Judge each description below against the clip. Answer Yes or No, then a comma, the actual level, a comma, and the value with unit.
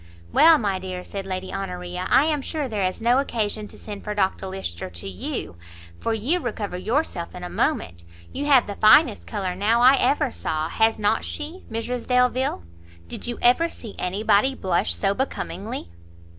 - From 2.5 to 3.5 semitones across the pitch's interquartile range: No, average, 5.3 semitones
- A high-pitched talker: Yes, high, 210 Hz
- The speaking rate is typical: Yes, average, 180 wpm